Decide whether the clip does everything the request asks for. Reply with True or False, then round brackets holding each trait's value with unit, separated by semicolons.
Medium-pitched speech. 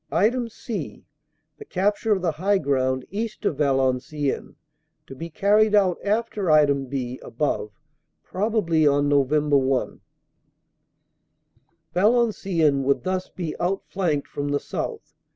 True (160 Hz)